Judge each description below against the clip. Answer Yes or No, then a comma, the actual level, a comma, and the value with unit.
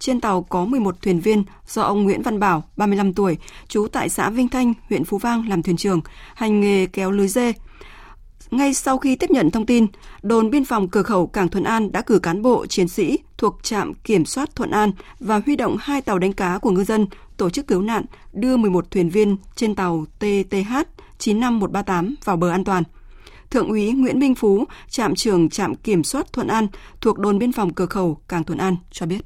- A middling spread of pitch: Yes, average, 4.0 semitones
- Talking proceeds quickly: No, average, 215 wpm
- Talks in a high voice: Yes, high, 205 Hz